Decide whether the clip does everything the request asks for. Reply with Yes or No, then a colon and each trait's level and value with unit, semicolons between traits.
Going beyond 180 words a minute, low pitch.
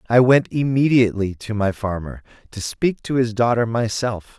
No: average, 165 wpm; low, 115 Hz